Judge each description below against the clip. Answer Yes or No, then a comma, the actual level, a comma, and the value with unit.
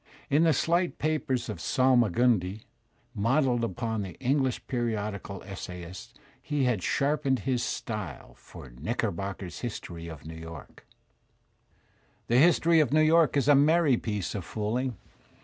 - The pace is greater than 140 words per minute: No, slow, 135 wpm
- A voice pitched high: No, low, 120 Hz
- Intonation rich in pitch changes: Yes, wide, 6.2 semitones